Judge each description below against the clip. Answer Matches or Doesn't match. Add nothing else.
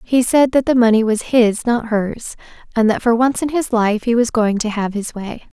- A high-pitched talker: Matches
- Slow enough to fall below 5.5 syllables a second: Matches